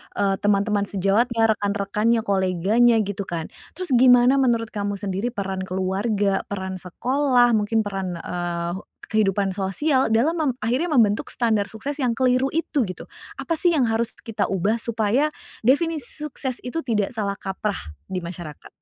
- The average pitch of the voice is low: No, high, 215 Hz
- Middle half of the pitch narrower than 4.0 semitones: No, average, 4.3 semitones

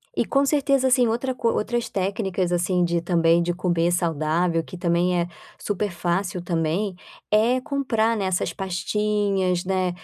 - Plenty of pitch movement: No, average, 3.8 semitones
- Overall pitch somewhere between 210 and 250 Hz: No, medium, 185 Hz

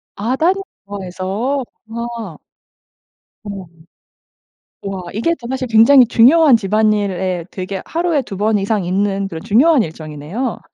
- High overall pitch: Yes, high, 215 Hz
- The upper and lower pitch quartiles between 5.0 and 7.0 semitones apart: No, average, 4.6 semitones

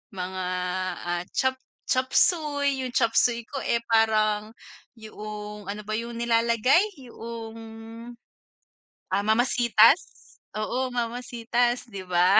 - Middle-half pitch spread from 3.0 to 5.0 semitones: No, narrow, 2.5 semitones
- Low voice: No, high, 230 Hz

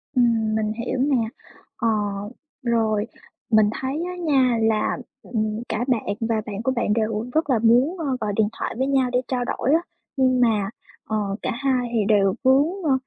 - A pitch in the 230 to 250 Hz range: Yes, high, 235 Hz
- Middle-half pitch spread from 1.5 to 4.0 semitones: Yes, average, 3.3 semitones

